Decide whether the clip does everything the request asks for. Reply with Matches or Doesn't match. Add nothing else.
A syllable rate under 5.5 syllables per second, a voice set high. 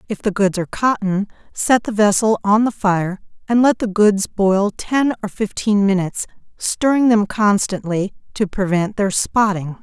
Matches